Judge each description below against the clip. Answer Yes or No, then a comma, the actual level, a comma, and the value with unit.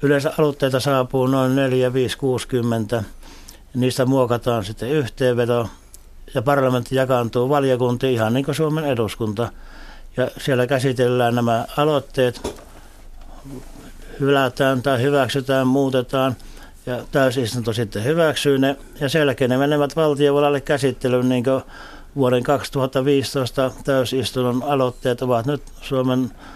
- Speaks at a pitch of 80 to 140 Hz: Yes, low, 130 Hz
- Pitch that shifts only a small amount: Yes, narrow, 2.1 semitones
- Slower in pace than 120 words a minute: Yes, average, 110 wpm